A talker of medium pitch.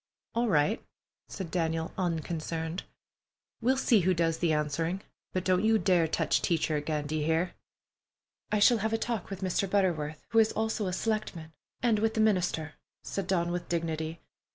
Yes: medium, 175 Hz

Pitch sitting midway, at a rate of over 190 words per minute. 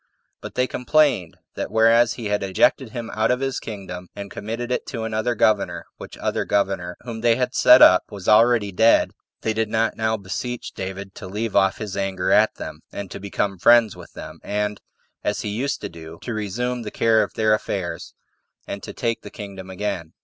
No: low, 110 Hz; average, 200 wpm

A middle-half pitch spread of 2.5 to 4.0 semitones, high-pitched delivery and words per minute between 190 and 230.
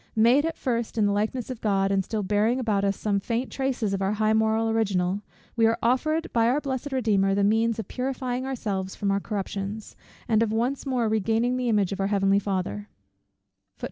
Yes: average, 3.5 semitones; high, 220 Hz; average, 200 wpm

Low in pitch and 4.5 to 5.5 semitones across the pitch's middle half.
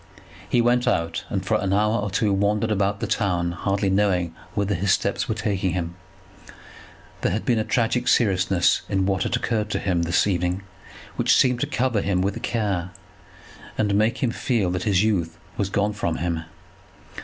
No: low, 100 Hz; average, 3.0 semitones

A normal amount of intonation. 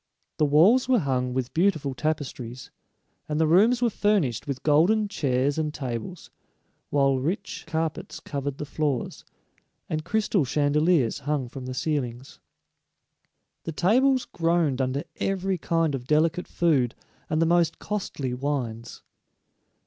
Yes: average, 4.6 semitones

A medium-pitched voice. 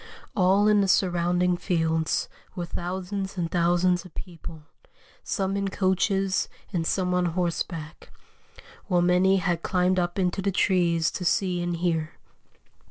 Yes: medium, 180 Hz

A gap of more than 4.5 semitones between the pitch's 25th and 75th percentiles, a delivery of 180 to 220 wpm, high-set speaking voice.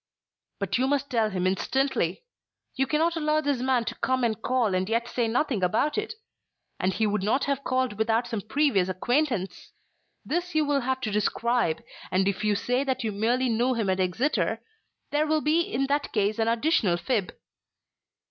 Yes: average, 4.9 semitones; average, 185 wpm; high, 240 Hz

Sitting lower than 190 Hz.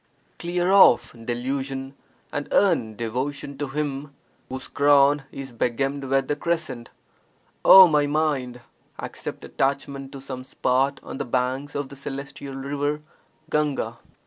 Yes: medium, 140 Hz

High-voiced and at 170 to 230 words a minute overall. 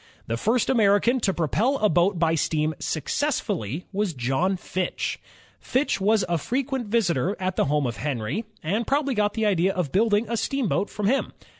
Yes: high, 200 Hz; average, 180 wpm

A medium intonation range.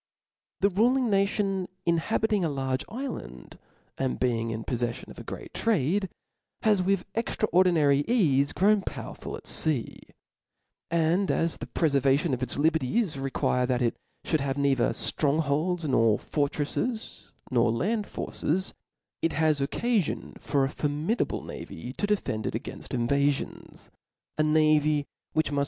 No: wide, 6.2 semitones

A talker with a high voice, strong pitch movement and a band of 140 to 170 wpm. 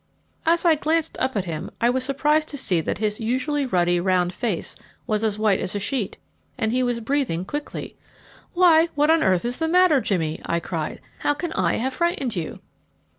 No: high, 245 Hz; wide, 7.8 semitones; average, 200 wpm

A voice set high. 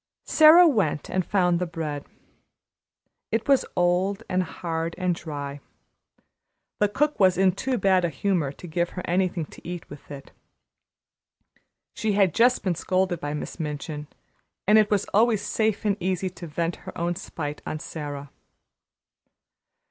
No: medium, 180 Hz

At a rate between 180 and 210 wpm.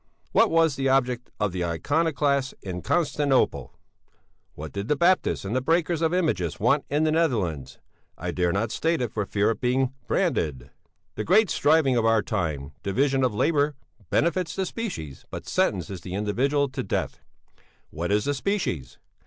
No: average, 165 wpm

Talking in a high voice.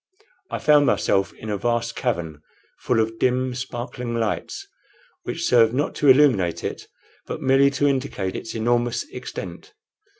No: low, 120 Hz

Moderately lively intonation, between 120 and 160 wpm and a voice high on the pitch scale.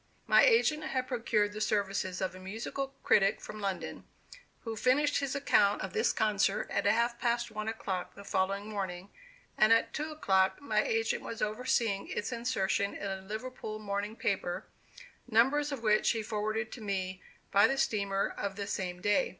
No: average, 3.2 semitones; average, 175 wpm; high, 215 Hz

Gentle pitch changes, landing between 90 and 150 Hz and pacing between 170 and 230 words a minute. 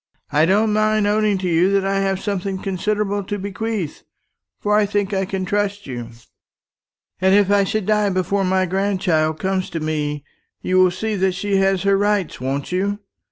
No: narrow, 1.9 semitones; high, 195 Hz; average, 185 wpm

